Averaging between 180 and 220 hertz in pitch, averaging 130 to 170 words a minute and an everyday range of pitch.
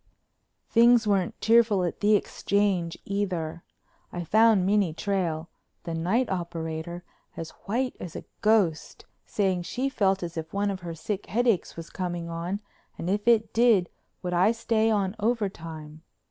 Yes: high, 190 Hz; average, 155 wpm; average, 4.1 semitones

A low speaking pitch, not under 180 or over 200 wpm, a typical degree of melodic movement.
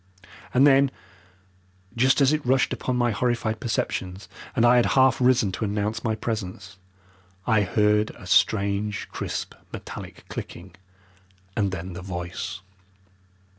No: low, 110 Hz; slow, 135 wpm; average, 4.0 semitones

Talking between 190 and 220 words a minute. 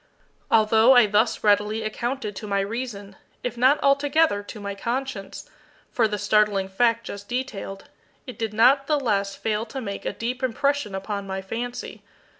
No: average, 165 wpm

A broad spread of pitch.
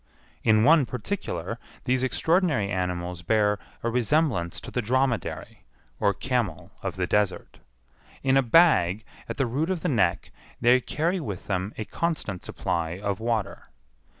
Yes: wide, 6.0 semitones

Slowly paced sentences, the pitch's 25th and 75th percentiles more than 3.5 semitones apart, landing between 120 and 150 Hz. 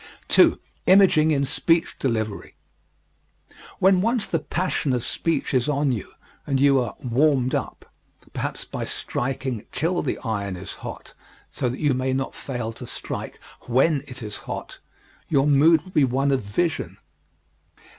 No: average, 155 wpm; average, 4.1 semitones; low, 135 Hz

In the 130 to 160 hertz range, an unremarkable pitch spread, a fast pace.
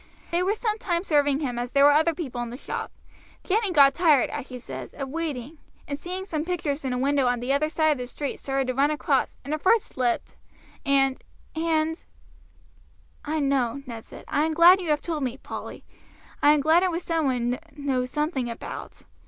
No: very high, 290 Hz; average, 3.7 semitones; fast, 220 wpm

